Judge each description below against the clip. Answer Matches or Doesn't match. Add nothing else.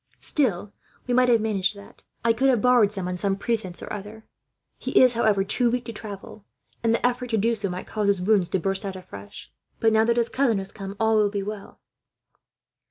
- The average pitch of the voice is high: Matches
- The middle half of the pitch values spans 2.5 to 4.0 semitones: Matches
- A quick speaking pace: Matches